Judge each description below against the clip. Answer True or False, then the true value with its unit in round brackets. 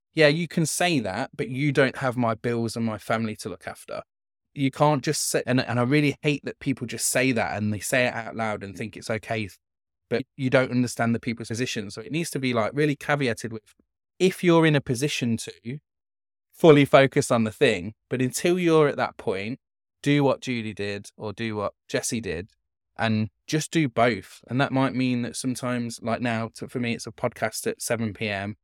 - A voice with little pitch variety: False (4.1 semitones)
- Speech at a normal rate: False (220 wpm)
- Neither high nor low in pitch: False (125 Hz)